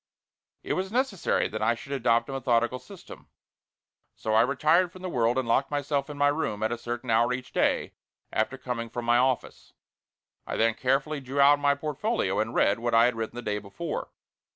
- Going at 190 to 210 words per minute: Yes, average, 200 wpm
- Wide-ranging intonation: No, average, 3.7 semitones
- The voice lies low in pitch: Yes, low, 125 Hz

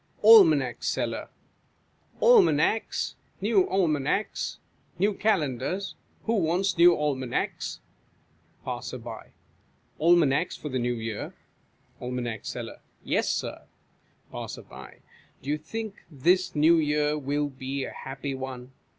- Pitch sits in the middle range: Yes, medium, 150 Hz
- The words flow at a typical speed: No, slow, 105 wpm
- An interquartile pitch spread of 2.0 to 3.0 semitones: No, wide, 5.6 semitones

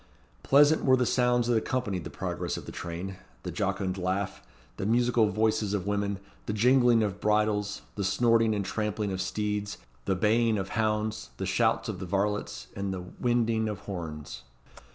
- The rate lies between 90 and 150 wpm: No, average, 175 wpm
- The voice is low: Yes, low, 105 Hz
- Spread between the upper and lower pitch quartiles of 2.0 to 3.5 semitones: Yes, average, 2.9 semitones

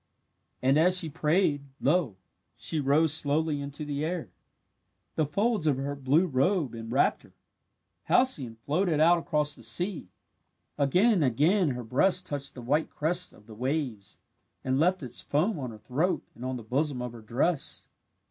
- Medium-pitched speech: Yes, medium, 145 Hz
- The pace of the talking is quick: No, average, 165 wpm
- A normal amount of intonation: Yes, average, 4.8 semitones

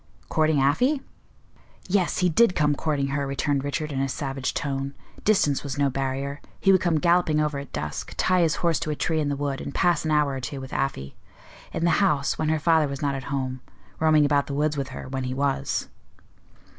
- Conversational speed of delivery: No, fast, 220 wpm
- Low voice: No, medium, 145 Hz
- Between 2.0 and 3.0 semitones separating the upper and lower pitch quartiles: Yes, narrow, 2.5 semitones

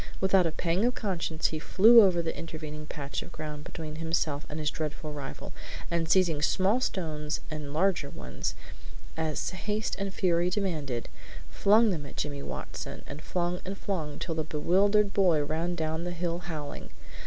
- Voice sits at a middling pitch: Yes, medium, 165 Hz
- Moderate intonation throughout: Yes, average, 3.7 semitones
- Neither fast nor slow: Yes, average, 170 wpm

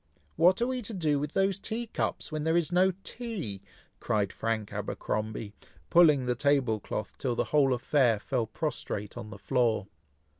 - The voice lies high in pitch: No, medium, 140 Hz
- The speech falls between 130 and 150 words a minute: No, average, 175 wpm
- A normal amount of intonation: No, wide, 7.9 semitones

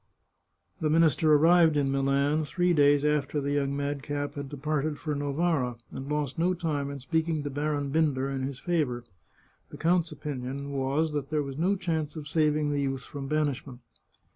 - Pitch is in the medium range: Yes, medium, 145 Hz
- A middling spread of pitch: No, narrow, 2.1 semitones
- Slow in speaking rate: No, average, 175 wpm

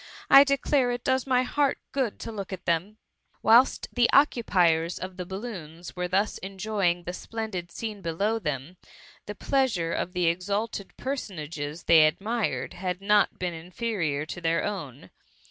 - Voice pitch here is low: No, high, 190 Hz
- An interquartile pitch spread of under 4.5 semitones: No, average, 5.0 semitones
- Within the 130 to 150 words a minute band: No, average, 160 wpm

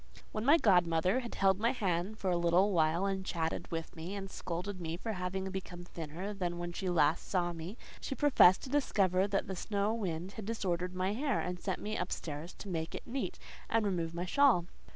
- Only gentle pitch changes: No, average, 3.0 semitones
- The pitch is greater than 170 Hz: Yes, medium, 185 Hz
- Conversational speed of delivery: No, fast, 215 wpm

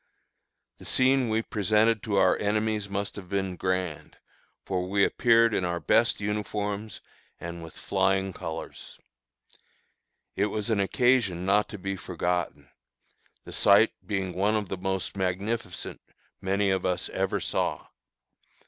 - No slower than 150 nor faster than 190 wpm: No, average, 140 wpm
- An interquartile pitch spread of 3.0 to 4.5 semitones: No, narrow, 2.4 semitones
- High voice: No, low, 100 Hz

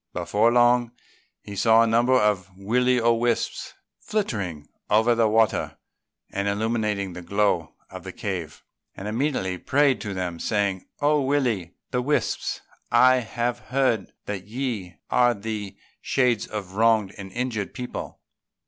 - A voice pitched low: Yes, low, 110 Hz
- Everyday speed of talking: Yes, average, 150 wpm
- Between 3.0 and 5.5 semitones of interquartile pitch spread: Yes, average, 3.7 semitones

